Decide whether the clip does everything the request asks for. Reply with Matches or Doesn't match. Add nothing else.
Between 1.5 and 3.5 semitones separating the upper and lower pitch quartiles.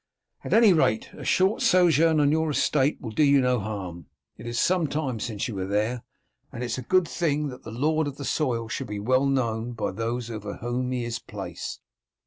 Doesn't match